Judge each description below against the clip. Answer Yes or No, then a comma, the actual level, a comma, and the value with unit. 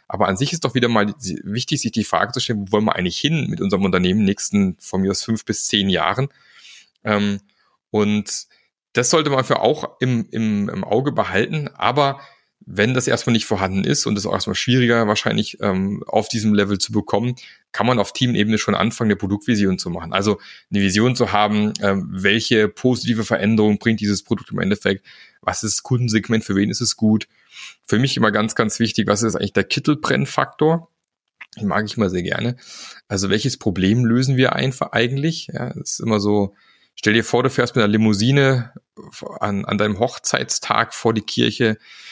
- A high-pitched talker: No, low, 110 Hz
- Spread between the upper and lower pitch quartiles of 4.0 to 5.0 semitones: No, average, 3.2 semitones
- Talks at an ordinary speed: No, fast, 195 wpm